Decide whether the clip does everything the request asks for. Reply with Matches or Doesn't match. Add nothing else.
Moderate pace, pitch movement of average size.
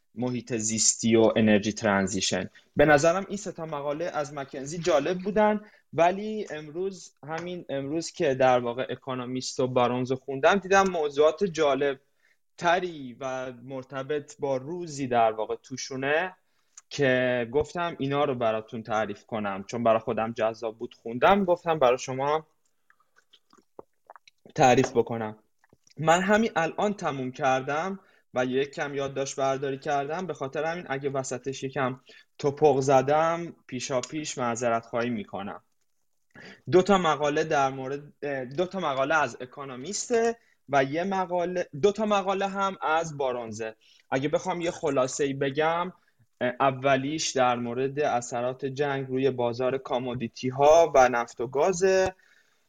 Matches